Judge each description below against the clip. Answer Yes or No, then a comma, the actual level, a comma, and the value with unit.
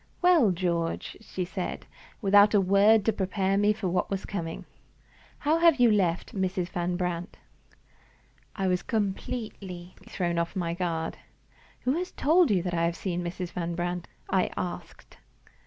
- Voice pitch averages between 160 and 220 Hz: Yes, medium, 185 Hz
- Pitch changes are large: No, average, 2.9 semitones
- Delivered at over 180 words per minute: No, average, 155 wpm